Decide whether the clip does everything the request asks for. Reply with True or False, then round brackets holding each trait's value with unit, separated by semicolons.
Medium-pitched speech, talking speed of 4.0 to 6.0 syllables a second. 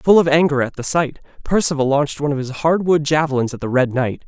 False (145 Hz; 6.3 syllables/s)